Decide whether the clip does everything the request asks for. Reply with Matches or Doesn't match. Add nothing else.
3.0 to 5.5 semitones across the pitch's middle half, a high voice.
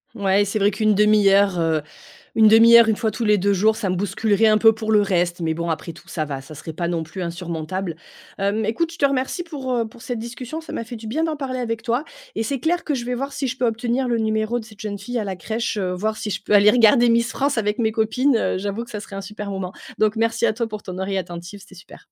Matches